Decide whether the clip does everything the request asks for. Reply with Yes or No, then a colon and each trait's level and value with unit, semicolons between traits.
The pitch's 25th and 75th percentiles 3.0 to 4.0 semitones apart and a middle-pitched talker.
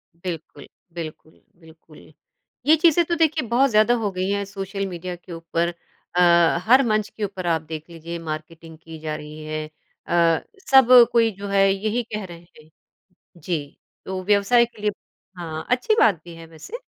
No: average, 4.6 semitones; medium, 180 Hz